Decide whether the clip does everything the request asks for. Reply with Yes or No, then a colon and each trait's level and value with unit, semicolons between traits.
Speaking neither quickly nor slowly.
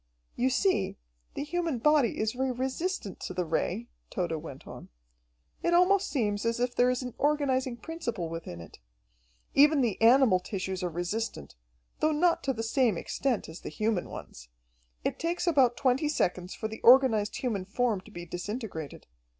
Yes: average, 170 wpm